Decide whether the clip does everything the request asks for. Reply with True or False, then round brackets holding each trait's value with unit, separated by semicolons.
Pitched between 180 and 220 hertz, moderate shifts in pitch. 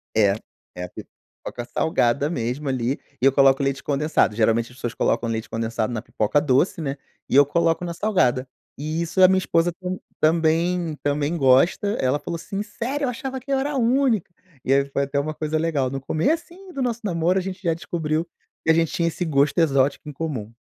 False (155 Hz; 5.0 semitones)